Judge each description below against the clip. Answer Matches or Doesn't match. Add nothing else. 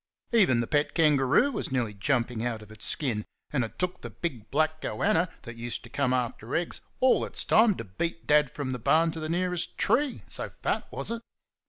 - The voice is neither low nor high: Matches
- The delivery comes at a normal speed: Doesn't match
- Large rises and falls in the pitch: Matches